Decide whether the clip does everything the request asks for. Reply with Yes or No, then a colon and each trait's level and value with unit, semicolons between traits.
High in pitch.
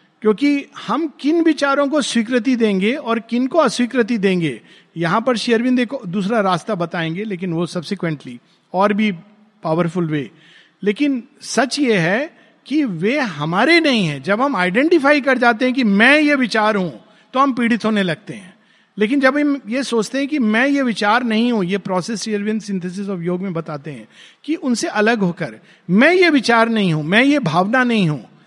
Yes: high, 220 Hz